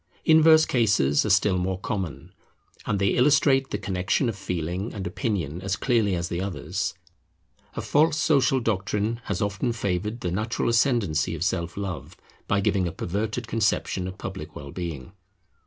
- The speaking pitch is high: No, low, 100 Hz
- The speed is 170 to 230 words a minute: No, average, 160 wpm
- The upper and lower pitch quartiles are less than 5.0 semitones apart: Yes, average, 4.3 semitones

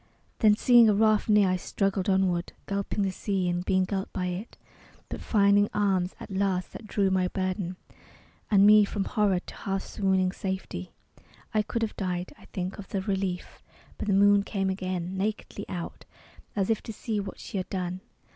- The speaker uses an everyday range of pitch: No, narrow, 1.8 semitones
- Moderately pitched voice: No, high, 195 Hz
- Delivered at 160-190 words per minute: Yes, average, 185 wpm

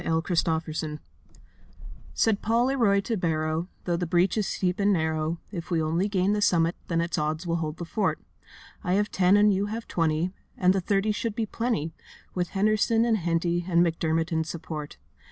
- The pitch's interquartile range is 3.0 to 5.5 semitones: Yes, average, 3.9 semitones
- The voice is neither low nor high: Yes, medium, 175 Hz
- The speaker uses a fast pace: No, average, 190 wpm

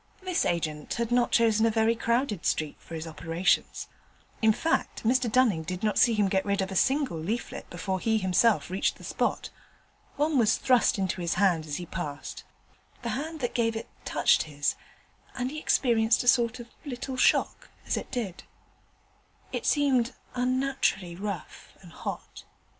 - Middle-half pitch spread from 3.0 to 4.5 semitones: No, wide, 5.5 semitones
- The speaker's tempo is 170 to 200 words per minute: Yes, average, 175 wpm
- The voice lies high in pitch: Yes, high, 220 Hz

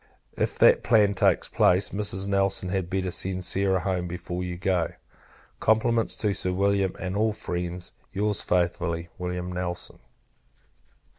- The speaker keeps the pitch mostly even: Yes, narrow, 1.9 semitones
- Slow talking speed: No, average, 150 wpm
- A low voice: Yes, very low, 95 Hz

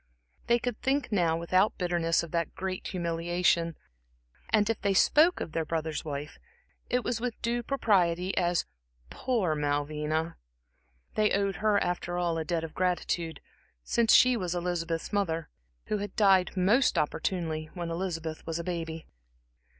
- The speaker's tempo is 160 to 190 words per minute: No, average, 150 wpm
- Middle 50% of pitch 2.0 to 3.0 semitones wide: No, average, 3.7 semitones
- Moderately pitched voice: Yes, medium, 175 Hz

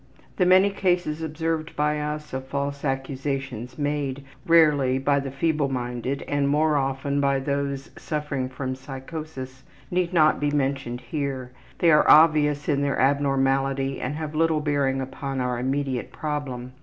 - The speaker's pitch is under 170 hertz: Yes, medium, 140 Hz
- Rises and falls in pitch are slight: Yes, narrow, 2.2 semitones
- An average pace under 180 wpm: Yes, average, 150 wpm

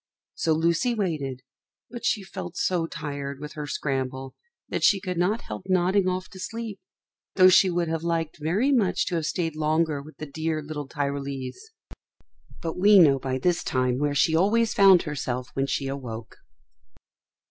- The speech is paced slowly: No, average, 170 wpm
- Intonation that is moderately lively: Yes, average, 4.8 semitones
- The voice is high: No, medium, 160 Hz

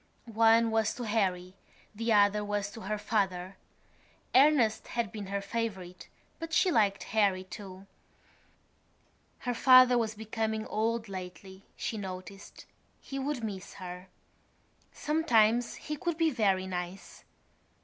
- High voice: Yes, high, 215 Hz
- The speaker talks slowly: Yes, slow, 130 wpm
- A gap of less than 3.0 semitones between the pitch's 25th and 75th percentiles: No, average, 3.3 semitones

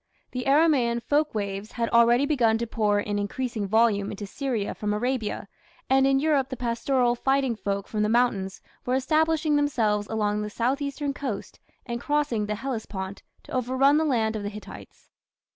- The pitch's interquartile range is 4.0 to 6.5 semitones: Yes, average, 4.4 semitones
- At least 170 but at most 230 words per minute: Yes, average, 175 wpm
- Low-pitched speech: No, high, 235 Hz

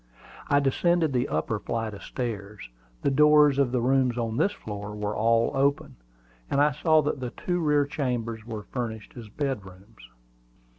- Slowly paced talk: No, average, 165 wpm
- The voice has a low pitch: Yes, low, 125 Hz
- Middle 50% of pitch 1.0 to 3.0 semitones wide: No, average, 4.7 semitones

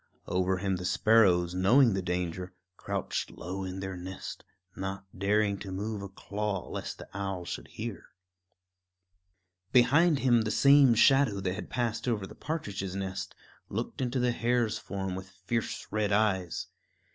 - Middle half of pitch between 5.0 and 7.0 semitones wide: No, average, 3.6 semitones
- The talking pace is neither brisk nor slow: Yes, average, 155 wpm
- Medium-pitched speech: No, low, 100 Hz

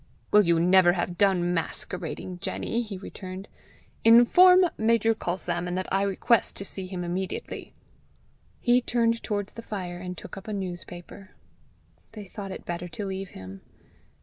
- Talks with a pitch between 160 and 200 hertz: Yes, high, 190 Hz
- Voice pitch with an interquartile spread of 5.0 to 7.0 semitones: No, average, 3.3 semitones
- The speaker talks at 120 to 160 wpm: Yes, average, 150 wpm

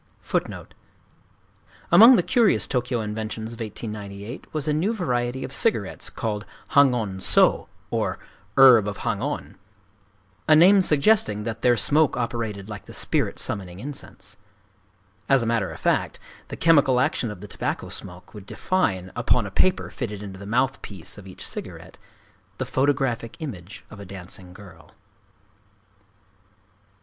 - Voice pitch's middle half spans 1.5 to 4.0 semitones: No, average, 5.3 semitones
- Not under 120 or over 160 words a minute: Yes, average, 140 wpm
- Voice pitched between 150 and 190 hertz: No, low, 110 Hz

